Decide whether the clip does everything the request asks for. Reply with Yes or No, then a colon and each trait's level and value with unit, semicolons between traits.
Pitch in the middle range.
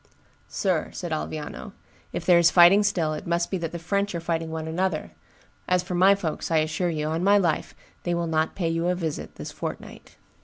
Yes: medium, 170 Hz